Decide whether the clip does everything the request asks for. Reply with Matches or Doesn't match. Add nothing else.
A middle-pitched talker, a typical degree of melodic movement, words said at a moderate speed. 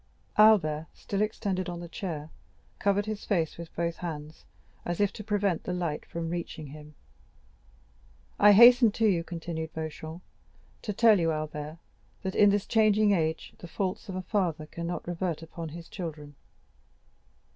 Matches